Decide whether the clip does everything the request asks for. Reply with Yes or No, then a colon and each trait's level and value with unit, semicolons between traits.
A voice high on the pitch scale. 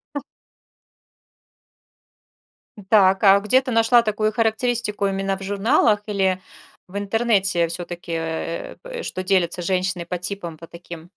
Yes: high, 195 Hz